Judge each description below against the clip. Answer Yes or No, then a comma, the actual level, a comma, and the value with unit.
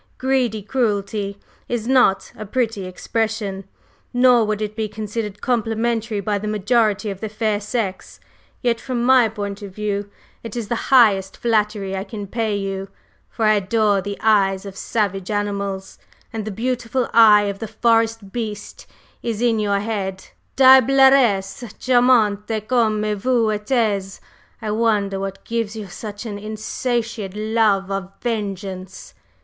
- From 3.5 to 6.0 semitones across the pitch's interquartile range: No, narrow, 2.5 semitones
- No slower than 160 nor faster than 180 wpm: No, average, 145 wpm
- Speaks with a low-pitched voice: No, high, 215 Hz